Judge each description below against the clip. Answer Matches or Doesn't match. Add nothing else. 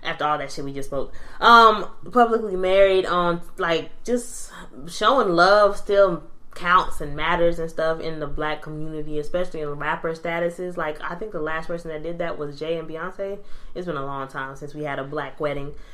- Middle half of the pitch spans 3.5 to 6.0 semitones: Doesn't match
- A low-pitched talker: Doesn't match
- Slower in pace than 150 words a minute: Doesn't match